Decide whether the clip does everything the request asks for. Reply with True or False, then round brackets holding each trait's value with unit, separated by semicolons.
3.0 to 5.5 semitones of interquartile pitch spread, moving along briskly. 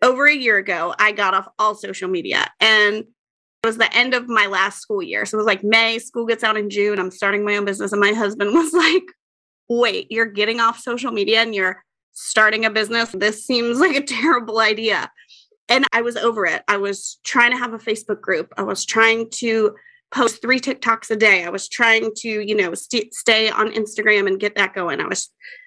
False (2.4 semitones; 220 wpm)